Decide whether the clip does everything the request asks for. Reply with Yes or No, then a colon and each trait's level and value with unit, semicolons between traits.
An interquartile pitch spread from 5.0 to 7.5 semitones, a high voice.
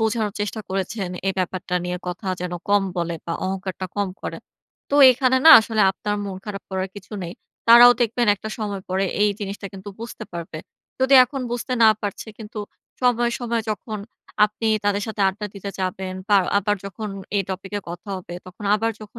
No: average, 2.8 semitones; high, 205 Hz